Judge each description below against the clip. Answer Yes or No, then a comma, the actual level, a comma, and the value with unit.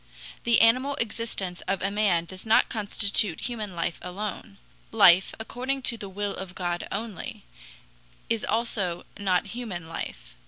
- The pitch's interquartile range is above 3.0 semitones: Yes, average, 4.0 semitones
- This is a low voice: No, high, 205 Hz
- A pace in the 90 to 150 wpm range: Yes, average, 145 wpm